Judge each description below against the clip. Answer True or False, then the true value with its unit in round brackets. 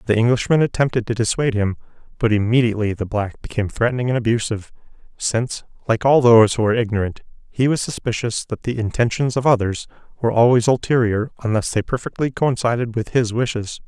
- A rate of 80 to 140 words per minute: False (170 wpm)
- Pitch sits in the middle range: False (115 Hz)